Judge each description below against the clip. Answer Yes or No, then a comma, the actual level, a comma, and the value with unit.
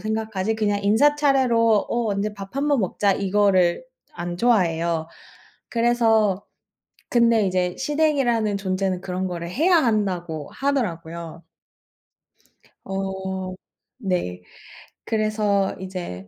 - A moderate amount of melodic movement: Yes, average, 4.0 semitones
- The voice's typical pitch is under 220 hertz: Yes, high, 200 Hz